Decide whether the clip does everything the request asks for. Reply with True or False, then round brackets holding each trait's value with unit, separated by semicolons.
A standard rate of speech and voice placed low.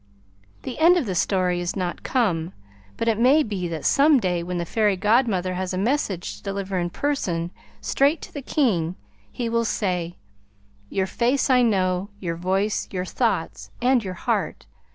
False (175 wpm; 195 Hz)